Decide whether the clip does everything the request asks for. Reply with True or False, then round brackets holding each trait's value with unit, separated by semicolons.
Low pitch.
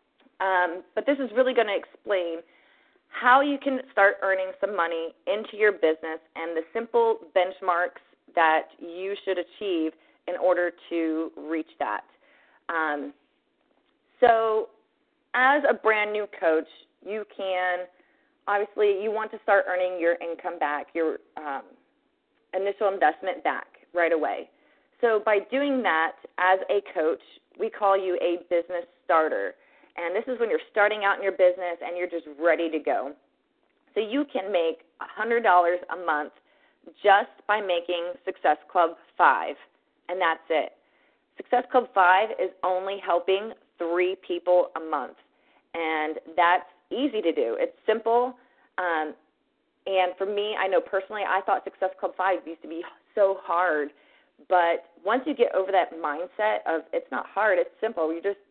False (190 Hz)